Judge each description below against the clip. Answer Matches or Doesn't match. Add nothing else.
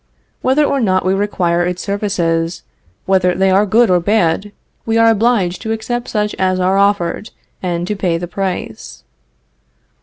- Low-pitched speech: Doesn't match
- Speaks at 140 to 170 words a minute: Matches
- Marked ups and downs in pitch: Doesn't match